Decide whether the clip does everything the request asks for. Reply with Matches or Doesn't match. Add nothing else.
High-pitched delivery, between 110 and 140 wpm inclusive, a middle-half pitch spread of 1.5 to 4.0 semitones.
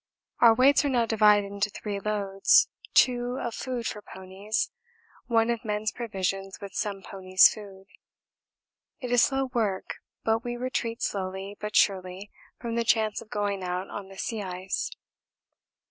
Doesn't match